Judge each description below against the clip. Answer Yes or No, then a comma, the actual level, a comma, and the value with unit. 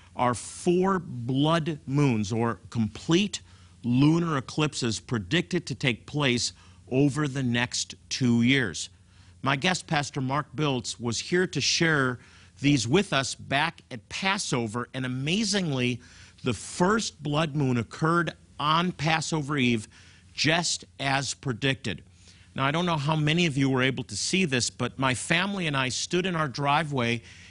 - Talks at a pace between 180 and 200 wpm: No, average, 145 wpm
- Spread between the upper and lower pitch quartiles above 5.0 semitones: Yes, wide, 5.5 semitones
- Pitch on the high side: No, low, 130 Hz